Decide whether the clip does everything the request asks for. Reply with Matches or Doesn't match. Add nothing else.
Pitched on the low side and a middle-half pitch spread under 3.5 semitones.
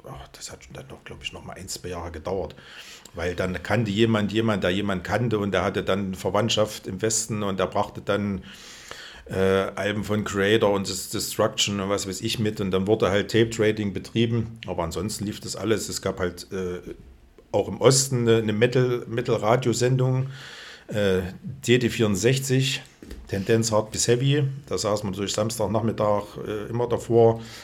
Matches